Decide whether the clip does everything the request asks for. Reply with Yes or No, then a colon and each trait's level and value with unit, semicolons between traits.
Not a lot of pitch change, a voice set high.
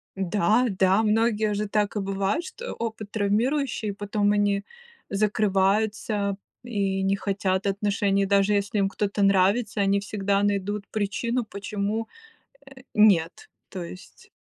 Yes: narrow, 1.4 semitones; high, 205 Hz